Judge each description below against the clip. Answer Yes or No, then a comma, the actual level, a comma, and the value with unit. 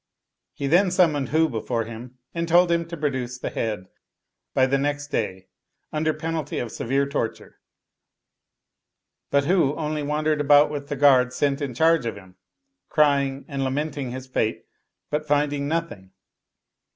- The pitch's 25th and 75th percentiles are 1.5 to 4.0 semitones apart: Yes, average, 3.2 semitones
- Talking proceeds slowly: No, average, 150 wpm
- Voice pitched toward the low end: No, medium, 145 Hz